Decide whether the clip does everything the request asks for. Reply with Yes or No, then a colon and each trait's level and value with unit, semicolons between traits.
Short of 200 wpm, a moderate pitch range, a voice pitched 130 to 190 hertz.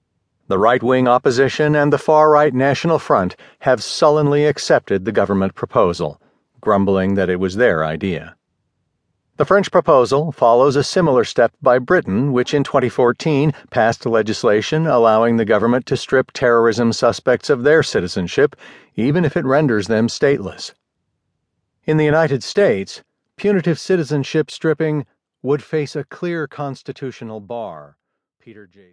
Yes: average, 140 wpm; average, 4.8 semitones; low, 135 Hz